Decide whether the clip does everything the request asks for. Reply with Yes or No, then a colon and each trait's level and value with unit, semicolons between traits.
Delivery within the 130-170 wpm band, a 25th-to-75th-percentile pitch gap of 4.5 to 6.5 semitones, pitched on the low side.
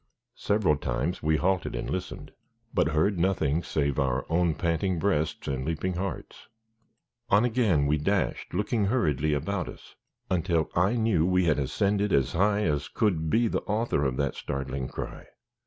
Yes: average, 160 wpm; average, 5.2 semitones; very low, 85 Hz